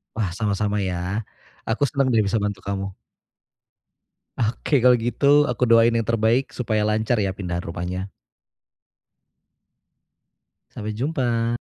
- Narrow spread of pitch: No, average, 3.0 semitones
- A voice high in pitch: No, low, 110 Hz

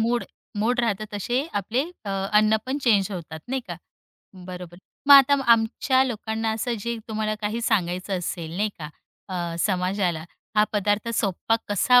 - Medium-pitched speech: No, high, 210 Hz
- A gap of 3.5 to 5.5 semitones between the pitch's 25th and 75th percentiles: Yes, average, 4.2 semitones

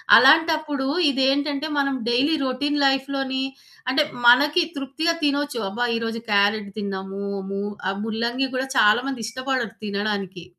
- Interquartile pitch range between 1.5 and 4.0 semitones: No, average, 4.7 semitones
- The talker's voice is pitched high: Yes, very high, 260 Hz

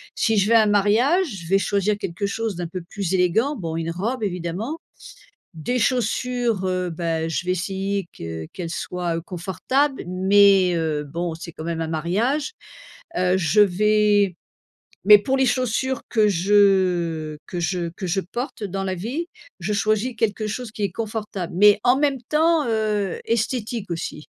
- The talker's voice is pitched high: Yes, high, 200 Hz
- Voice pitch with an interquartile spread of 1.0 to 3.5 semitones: No, average, 4.3 semitones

